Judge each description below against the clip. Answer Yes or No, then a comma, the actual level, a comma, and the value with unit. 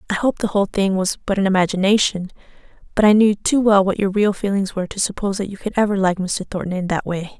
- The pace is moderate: No, fast, 250 wpm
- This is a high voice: Yes, high, 200 Hz